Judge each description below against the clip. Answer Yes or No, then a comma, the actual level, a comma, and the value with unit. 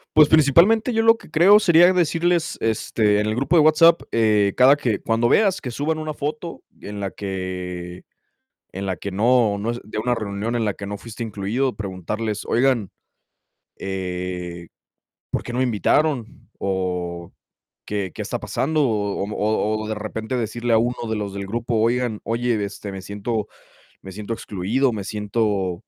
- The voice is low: Yes, low, 110 Hz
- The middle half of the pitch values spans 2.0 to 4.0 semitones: No, average, 4.5 semitones